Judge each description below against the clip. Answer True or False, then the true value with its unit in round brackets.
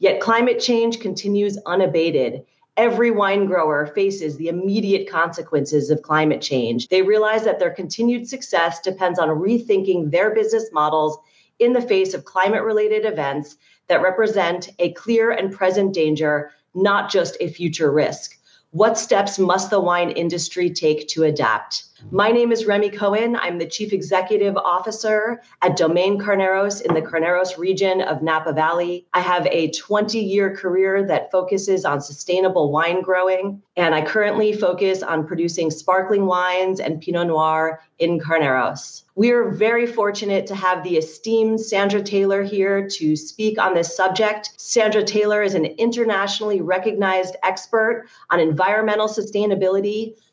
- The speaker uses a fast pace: False (150 wpm)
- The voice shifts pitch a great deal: False (3.8 semitones)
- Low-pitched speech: False (190 Hz)